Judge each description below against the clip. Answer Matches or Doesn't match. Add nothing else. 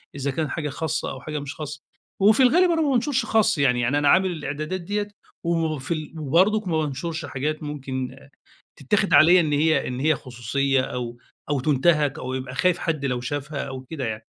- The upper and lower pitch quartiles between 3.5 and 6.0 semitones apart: Matches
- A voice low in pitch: Doesn't match